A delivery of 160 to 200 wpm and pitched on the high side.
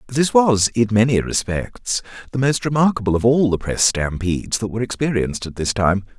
No: average, 185 wpm; low, 115 Hz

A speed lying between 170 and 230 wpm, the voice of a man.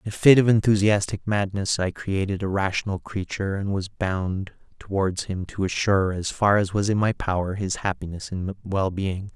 Yes: average, 185 wpm; male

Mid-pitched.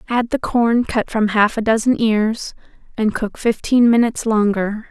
No: high, 225 Hz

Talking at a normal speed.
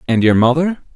Yes: average, 190 wpm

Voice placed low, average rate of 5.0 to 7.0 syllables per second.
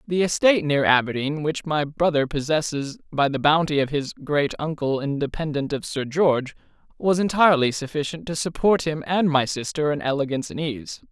No: medium, 150 Hz; 5.3 syllables/s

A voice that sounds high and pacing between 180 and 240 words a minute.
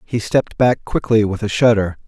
No: low, 110 Hz; average, 200 wpm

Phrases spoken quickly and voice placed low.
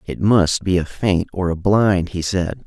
Yes: fast, 225 wpm; very low, 90 Hz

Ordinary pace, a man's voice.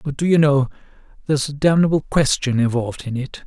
Yes: average, 190 wpm; male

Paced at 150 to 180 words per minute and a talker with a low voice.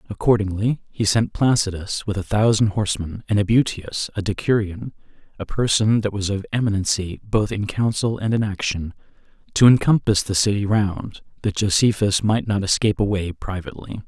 Yes: average, 155 wpm; low, 105 Hz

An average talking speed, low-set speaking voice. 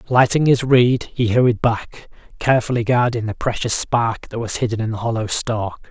Yes: average, 185 wpm; low, 115 Hz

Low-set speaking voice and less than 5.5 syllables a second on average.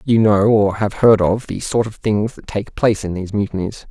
Yes: low, 105 Hz; 5.3 syllables/s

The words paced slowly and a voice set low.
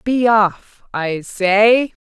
No: slow, 120 wpm; high, 210 Hz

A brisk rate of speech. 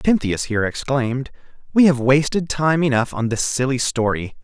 No: average, 160 wpm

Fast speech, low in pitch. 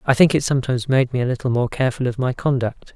Yes: fast, 265 wpm; low, 130 Hz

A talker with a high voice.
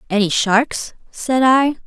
Yes: high, 240 Hz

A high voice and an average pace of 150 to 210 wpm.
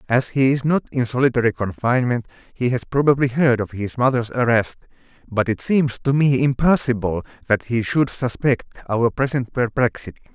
No: low, 125 Hz; average, 160 wpm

